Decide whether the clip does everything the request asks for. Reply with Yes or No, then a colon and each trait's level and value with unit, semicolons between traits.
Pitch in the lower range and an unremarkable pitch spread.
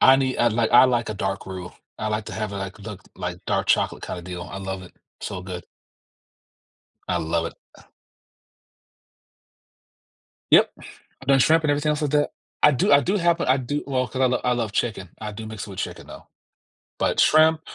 No: low, 110 Hz; wide, 6.1 semitones